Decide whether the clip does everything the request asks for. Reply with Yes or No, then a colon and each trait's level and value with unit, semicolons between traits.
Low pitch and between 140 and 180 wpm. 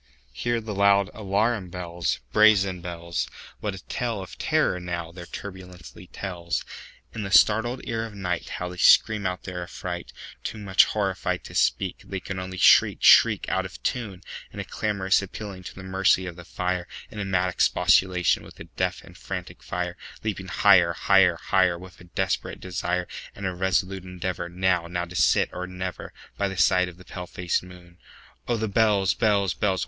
Yes: very low, 95 Hz; average, 155 wpm